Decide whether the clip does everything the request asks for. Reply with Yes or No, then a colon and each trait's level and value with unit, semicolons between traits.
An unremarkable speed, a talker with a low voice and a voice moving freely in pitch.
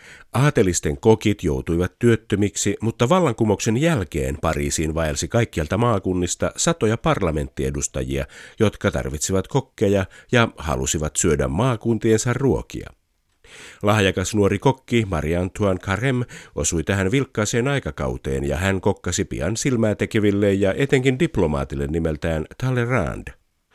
Yes: average, 105 wpm; low, 100 Hz; wide, 6.3 semitones